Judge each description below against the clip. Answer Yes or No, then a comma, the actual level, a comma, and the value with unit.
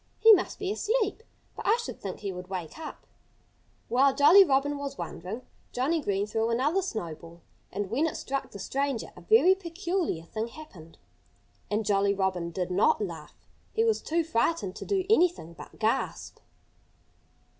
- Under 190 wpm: Yes, average, 160 wpm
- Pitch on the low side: No, very high, 255 Hz